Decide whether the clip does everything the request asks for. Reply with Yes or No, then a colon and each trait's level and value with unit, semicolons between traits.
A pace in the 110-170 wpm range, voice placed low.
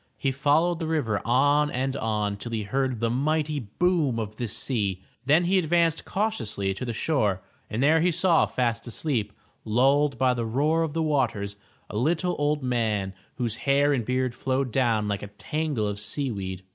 No: average, 185 wpm; low, 130 Hz